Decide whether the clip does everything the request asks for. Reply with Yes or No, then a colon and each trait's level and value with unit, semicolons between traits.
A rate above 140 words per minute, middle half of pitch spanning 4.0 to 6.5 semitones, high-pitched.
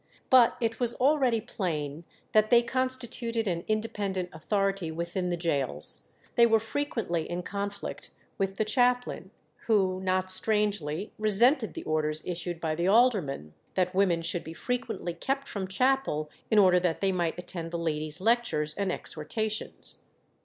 Yes: average, 150 wpm; average, 5.1 semitones; high, 195 Hz